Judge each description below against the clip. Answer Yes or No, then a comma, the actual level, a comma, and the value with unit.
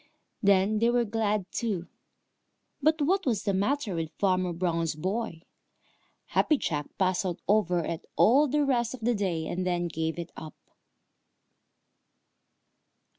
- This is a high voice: Yes, high, 195 Hz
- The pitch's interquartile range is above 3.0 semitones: Yes, average, 5.3 semitones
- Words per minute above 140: No, slow, 135 wpm